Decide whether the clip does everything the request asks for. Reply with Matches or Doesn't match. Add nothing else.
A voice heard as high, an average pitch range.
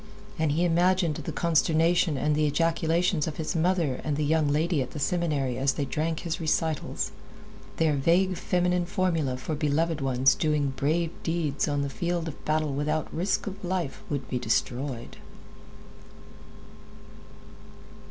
Doesn't match